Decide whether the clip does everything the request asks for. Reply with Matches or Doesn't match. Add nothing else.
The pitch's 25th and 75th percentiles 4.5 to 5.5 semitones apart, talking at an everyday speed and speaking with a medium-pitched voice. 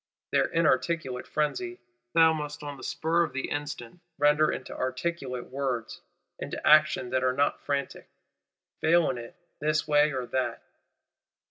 Doesn't match